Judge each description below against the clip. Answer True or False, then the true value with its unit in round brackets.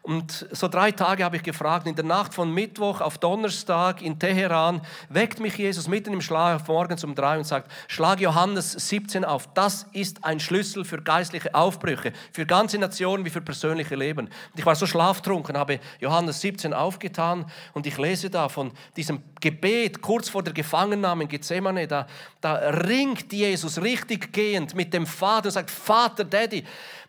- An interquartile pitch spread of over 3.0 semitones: True (3.7 semitones)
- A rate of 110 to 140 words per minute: False (175 wpm)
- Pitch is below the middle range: False (175 Hz)